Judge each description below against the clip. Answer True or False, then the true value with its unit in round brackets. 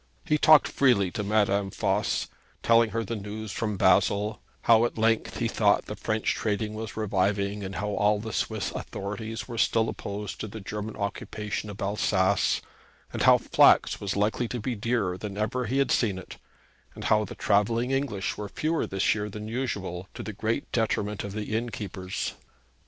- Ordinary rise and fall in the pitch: False (2.0 semitones)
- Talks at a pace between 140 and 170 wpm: False (180 wpm)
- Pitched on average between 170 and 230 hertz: False (105 Hz)